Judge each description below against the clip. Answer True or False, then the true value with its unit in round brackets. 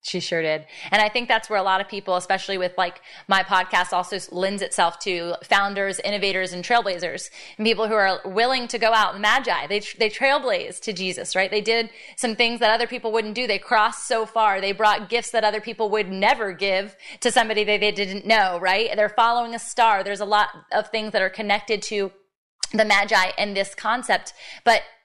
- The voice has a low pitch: False (210 Hz)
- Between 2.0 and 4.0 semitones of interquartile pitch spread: True (2.7 semitones)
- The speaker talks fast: True (215 wpm)